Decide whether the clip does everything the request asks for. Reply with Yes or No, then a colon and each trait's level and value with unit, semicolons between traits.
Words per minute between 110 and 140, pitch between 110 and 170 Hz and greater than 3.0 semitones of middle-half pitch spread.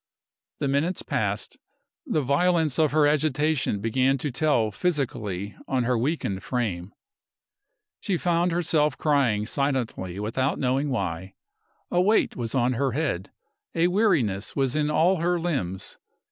Yes: slow, 135 wpm; medium, 140 Hz; wide, 5.6 semitones